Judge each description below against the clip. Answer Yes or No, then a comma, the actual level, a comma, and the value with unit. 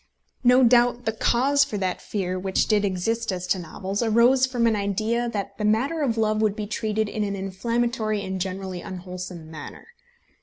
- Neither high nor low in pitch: No, high, 215 Hz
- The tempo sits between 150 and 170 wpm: No, average, 185 wpm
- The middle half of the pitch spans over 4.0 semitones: No, average, 3.6 semitones